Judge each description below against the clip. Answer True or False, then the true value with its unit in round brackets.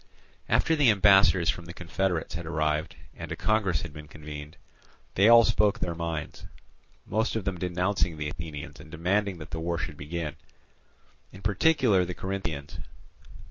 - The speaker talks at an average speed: True (160 wpm)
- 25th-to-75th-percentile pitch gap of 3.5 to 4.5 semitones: True (3.9 semitones)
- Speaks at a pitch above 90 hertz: False (85 Hz)